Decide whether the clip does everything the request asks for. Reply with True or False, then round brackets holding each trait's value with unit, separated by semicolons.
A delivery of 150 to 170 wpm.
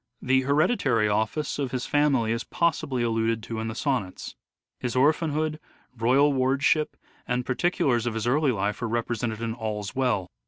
True (165 wpm)